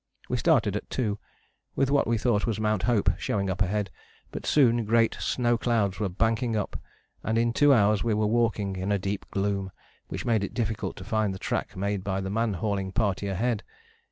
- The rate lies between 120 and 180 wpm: No, fast, 205 wpm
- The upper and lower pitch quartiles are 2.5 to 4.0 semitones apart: Yes, average, 2.8 semitones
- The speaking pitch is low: Yes, low, 105 Hz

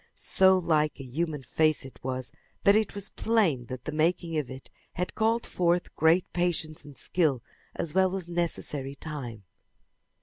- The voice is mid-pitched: Yes, medium, 160 Hz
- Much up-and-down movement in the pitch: No, average, 4.6 semitones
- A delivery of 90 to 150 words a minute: No, average, 165 wpm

